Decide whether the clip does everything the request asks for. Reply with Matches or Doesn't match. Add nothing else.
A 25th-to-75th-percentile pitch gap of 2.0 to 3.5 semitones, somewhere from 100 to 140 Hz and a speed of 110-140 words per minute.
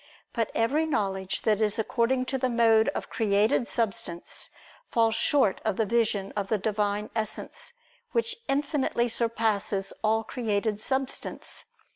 Doesn't match